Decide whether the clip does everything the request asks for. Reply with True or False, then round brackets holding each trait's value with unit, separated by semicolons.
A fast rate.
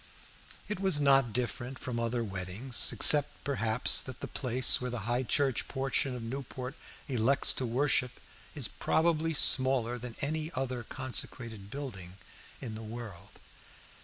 False (140 wpm)